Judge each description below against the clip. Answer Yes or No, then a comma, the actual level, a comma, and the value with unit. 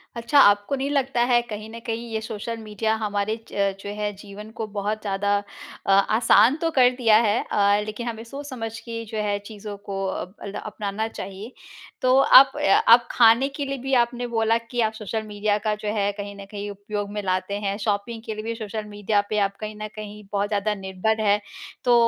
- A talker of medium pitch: No, high, 215 Hz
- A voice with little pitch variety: Yes, narrow, 2.2 semitones